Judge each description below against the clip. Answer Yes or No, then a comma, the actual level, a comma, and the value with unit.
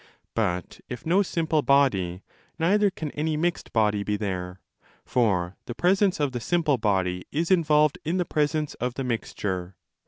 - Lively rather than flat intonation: Yes, wide, 8.1 semitones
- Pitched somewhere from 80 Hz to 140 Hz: Yes, low, 135 Hz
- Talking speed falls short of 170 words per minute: Yes, average, 160 wpm